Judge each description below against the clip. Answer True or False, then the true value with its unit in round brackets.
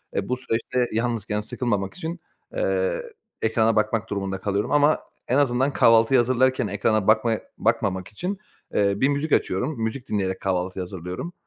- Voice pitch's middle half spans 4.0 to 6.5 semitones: True (4.5 semitones)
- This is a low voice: True (115 Hz)